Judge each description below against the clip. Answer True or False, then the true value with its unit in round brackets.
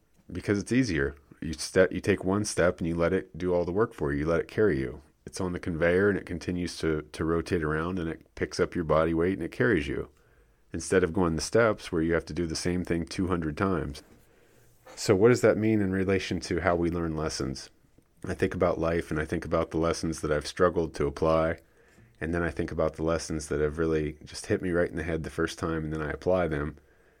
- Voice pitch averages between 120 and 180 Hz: False (85 Hz)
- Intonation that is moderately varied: False (2.2 semitones)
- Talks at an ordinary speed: False (250 wpm)